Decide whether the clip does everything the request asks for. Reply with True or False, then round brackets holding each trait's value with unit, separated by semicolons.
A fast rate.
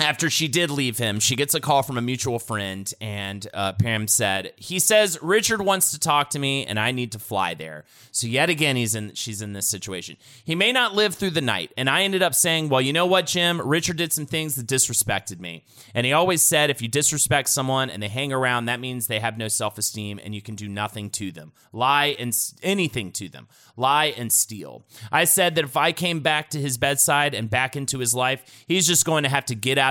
True (245 wpm)